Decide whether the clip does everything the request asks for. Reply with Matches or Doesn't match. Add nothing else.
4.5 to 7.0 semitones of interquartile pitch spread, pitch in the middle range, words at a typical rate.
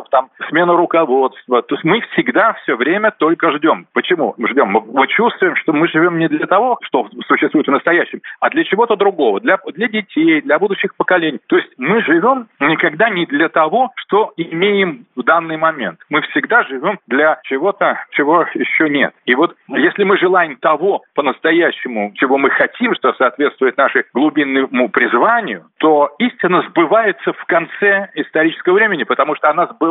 Doesn't match